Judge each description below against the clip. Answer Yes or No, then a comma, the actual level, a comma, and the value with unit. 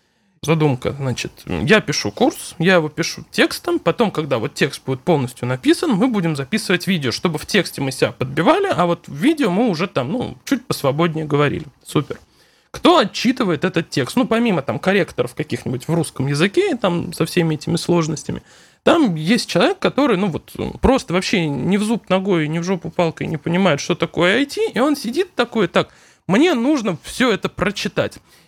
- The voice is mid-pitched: Yes, medium, 175 Hz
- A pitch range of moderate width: No, wide, 6.3 semitones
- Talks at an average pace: No, fast, 180 wpm